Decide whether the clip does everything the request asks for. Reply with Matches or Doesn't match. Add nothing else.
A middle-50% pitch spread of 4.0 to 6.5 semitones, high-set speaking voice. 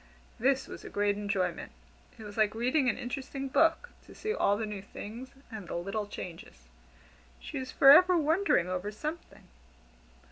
Matches